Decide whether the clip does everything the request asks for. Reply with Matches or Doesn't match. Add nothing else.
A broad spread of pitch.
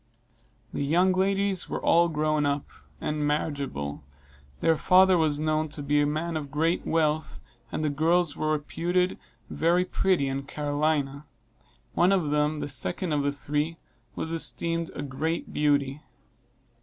Doesn't match